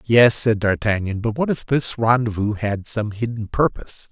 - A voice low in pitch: Yes, low, 115 Hz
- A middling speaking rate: Yes, average, 175 wpm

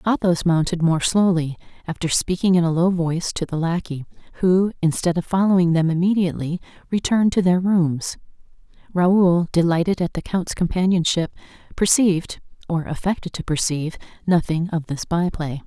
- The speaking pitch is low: No, medium, 175 Hz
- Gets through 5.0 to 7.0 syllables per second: Yes, 5.3 syllables/s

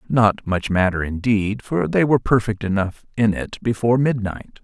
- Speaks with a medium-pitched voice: No, low, 110 Hz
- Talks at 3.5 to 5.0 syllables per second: Yes, 4.8 syllables/s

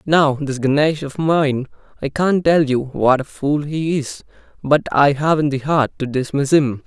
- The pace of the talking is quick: No, average, 185 wpm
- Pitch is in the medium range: Yes, medium, 145 Hz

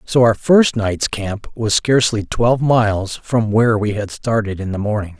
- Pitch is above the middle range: No, low, 110 Hz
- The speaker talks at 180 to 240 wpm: Yes, average, 195 wpm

